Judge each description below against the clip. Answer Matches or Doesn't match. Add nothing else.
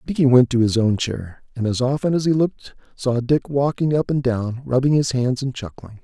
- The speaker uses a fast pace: Matches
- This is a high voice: Doesn't match